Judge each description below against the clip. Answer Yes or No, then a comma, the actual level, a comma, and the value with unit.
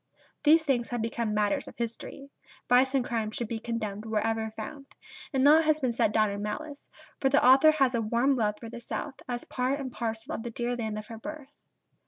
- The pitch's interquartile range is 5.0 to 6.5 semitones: No, average, 3.6 semitones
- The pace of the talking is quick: Yes, fast, 220 wpm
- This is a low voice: No, high, 240 Hz